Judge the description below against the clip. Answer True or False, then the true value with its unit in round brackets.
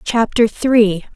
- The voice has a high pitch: True (220 Hz)